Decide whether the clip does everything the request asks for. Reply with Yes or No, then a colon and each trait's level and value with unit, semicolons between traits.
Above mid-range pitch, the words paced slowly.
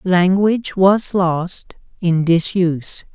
No: medium, 180 Hz; slow, 95 wpm